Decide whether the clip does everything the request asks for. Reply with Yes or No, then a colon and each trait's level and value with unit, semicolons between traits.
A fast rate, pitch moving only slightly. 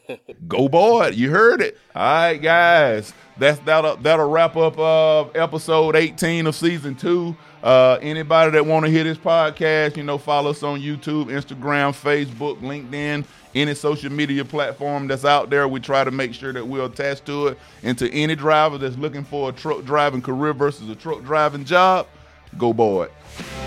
No: average, 180 wpm; narrow, 2.3 semitones